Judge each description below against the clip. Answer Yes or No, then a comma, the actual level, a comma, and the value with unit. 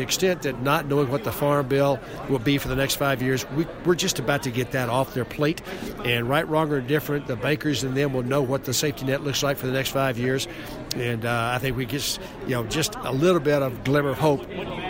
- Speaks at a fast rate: Yes, fast, 255 wpm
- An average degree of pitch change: No, narrow, 2.1 semitones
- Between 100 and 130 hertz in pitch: No, medium, 140 Hz